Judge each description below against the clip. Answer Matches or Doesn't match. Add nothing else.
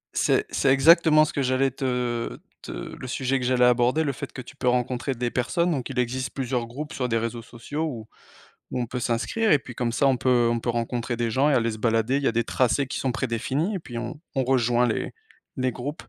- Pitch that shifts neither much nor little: Doesn't match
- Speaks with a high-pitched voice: Doesn't match